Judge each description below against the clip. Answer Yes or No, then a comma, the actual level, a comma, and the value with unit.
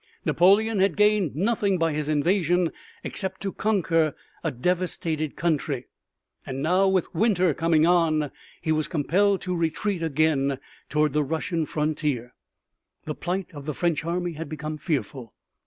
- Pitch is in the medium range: Yes, medium, 165 Hz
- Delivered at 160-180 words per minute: No, average, 145 wpm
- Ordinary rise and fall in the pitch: Yes, average, 3.3 semitones